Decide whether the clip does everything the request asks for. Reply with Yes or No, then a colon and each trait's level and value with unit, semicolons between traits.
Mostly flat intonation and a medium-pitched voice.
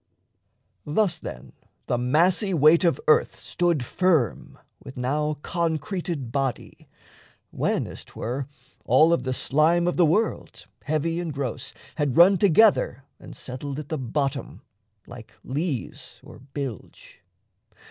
No: average, 4.4 semitones; medium, 150 Hz